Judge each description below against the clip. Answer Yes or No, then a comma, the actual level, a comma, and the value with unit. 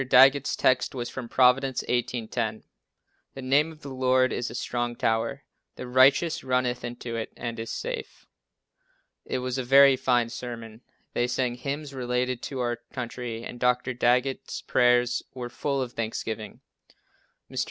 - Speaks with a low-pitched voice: Yes, low, 125 Hz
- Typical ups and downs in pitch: No, narrow, 1.6 semitones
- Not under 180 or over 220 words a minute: No, average, 155 wpm